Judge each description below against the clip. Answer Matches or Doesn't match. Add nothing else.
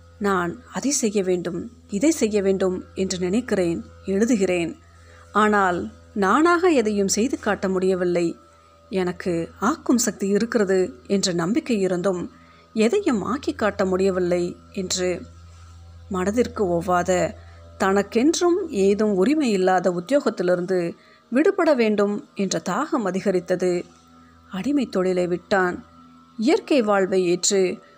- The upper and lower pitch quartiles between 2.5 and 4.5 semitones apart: Matches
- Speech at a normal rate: Matches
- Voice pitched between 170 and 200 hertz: Matches